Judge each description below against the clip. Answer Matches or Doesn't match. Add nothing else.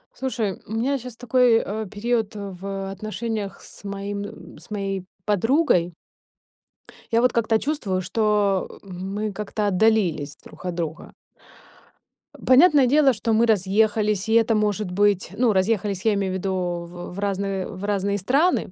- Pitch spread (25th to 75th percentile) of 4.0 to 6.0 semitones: Doesn't match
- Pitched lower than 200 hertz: Doesn't match